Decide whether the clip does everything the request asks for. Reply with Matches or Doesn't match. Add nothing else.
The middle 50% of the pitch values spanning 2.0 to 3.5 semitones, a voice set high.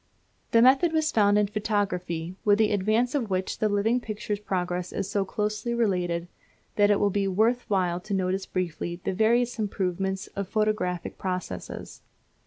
Matches